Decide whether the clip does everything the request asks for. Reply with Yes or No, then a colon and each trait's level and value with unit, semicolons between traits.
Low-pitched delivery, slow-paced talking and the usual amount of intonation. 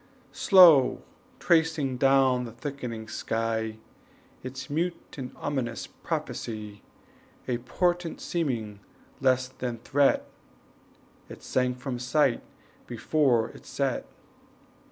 Yes: low, 130 Hz; slow, 95 wpm; average, 3.6 semitones